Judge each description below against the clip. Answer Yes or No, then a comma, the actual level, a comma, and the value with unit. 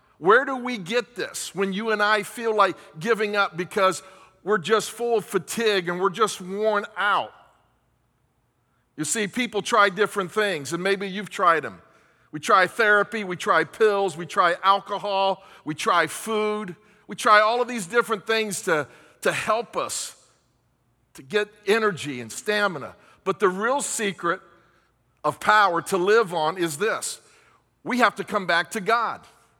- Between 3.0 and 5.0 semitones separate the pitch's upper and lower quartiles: Yes, average, 3.6 semitones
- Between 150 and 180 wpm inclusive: Yes, average, 165 wpm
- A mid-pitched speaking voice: No, high, 200 Hz